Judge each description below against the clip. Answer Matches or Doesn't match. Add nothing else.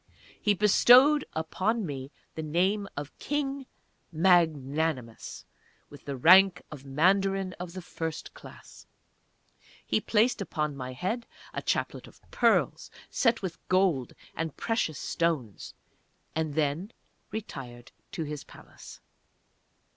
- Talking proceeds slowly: Matches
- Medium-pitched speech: Matches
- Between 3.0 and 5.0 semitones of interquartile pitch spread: Doesn't match